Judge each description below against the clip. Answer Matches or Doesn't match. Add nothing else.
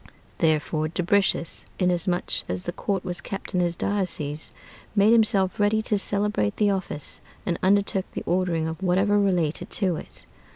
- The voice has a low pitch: Doesn't match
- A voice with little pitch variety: Doesn't match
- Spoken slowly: Doesn't match